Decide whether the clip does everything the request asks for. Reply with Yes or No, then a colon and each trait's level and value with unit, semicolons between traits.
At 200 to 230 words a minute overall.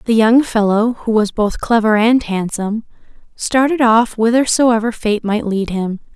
No: average, 155 wpm